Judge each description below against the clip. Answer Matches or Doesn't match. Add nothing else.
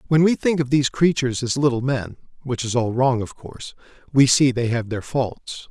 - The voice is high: Doesn't match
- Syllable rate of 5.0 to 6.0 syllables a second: Doesn't match